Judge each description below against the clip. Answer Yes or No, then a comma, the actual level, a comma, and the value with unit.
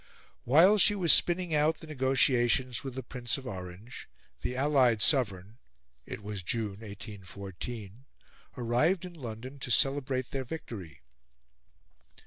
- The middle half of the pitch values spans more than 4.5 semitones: Yes, average, 4.9 semitones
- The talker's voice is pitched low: Yes, low, 125 Hz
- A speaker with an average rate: No, slow, 125 wpm